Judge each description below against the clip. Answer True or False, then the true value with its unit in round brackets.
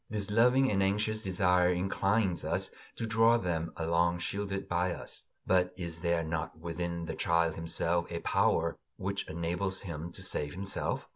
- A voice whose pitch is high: False (90 Hz)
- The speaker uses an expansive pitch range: False (2.8 semitones)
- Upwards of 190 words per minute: False (160 wpm)